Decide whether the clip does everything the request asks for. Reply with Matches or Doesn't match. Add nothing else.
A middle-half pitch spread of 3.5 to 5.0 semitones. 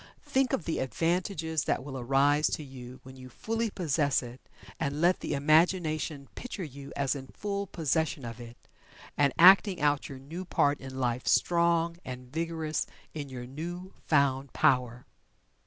Matches